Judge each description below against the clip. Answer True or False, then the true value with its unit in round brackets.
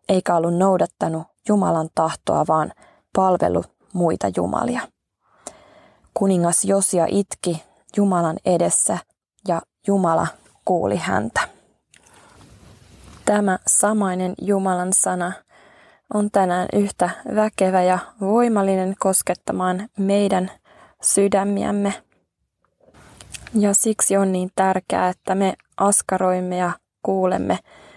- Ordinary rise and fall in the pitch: False (1.8 semitones)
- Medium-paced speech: False (90 wpm)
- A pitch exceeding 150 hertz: True (190 Hz)